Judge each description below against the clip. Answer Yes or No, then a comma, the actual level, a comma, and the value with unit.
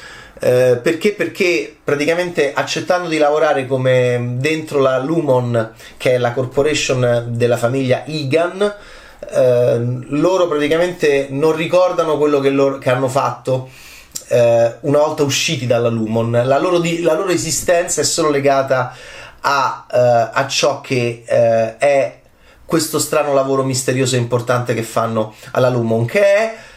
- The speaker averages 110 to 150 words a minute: Yes, average, 140 wpm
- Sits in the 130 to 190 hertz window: Yes, low, 135 Hz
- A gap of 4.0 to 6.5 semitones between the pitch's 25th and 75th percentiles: Yes, average, 4.3 semitones